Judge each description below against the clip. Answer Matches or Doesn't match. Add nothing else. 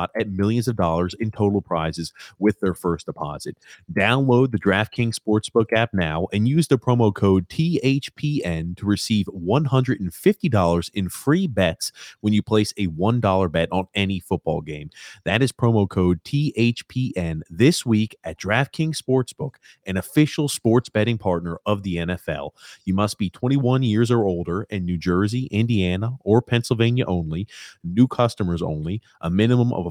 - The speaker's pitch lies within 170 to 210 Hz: Doesn't match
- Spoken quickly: Doesn't match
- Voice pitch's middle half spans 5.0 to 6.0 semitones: Matches